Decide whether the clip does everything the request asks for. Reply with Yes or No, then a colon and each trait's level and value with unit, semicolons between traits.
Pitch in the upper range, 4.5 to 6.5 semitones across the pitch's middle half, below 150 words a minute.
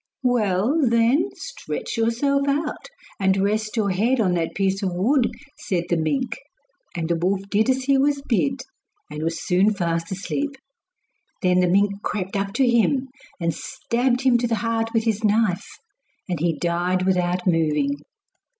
No: high, 205 Hz; average, 5.2 semitones; average, 165 wpm